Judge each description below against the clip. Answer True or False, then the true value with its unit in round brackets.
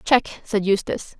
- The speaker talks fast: False (150 wpm)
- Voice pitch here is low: False (210 Hz)